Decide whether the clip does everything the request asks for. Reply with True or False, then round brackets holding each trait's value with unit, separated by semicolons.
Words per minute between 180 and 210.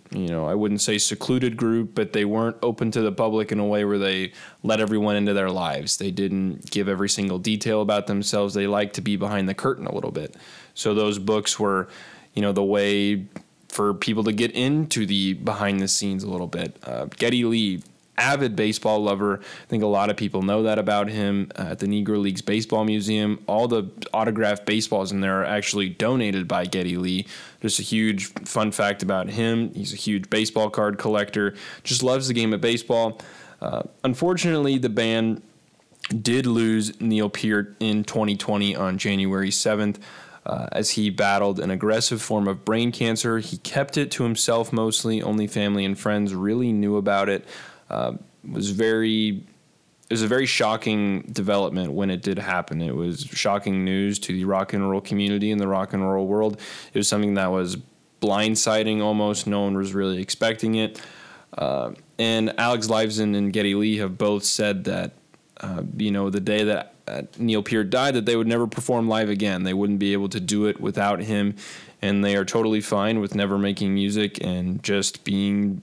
True (195 wpm)